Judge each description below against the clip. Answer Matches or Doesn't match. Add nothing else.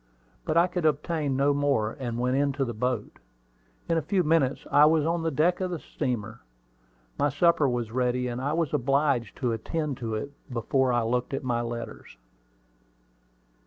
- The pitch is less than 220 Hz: Matches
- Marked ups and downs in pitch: Doesn't match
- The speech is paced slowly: Doesn't match